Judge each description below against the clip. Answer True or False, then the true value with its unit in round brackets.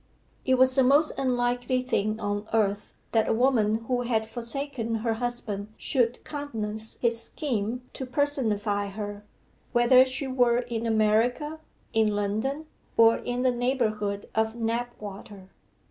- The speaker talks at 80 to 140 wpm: True (135 wpm)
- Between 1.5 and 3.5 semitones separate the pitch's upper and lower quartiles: True (2.9 semitones)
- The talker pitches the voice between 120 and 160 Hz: False (235 Hz)